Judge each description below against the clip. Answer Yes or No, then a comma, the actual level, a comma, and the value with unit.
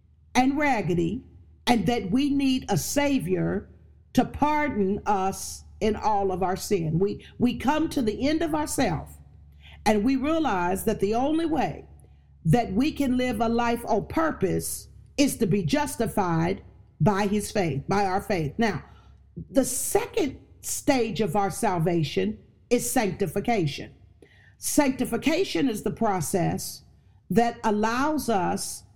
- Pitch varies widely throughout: Yes, wide, 6.1 semitones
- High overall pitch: Yes, high, 220 Hz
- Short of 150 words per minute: Yes, slow, 135 wpm